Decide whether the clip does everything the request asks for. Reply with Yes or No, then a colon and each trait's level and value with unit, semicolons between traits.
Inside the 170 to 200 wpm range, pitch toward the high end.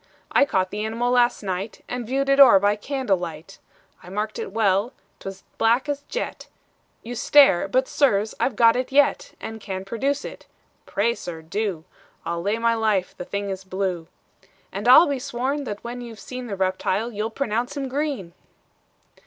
Yes: average, 180 wpm; high, 225 Hz